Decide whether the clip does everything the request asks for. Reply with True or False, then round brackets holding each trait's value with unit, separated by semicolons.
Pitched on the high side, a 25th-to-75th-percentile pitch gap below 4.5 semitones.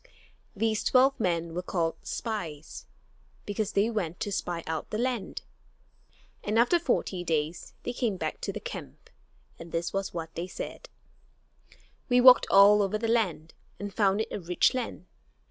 False (195 Hz; 5.0 semitones)